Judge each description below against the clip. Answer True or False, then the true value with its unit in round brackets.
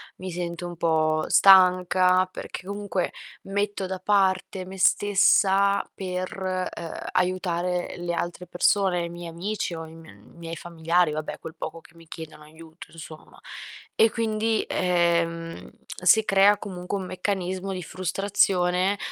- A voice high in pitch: False (180 Hz)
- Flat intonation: True (2.3 semitones)